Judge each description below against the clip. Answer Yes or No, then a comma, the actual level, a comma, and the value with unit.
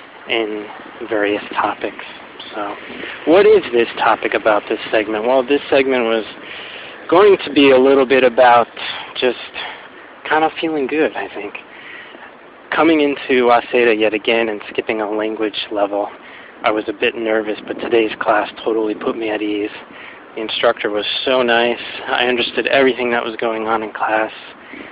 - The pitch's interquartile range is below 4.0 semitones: Yes, average, 3.3 semitones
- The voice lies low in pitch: Yes, low, 115 Hz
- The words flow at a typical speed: Yes, average, 160 wpm